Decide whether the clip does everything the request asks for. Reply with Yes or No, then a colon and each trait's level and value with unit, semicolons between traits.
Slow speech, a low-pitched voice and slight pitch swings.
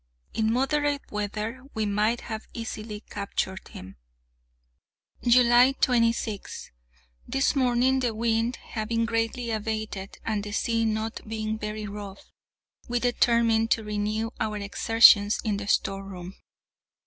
No: slow, 120 wpm; high, 220 Hz; narrow, 2.1 semitones